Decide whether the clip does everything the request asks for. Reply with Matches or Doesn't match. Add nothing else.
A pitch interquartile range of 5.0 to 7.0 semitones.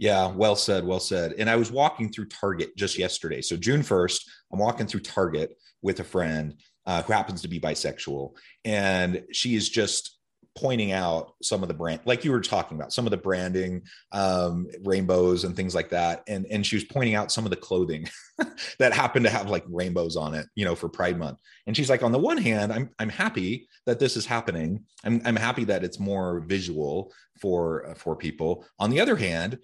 Doesn't match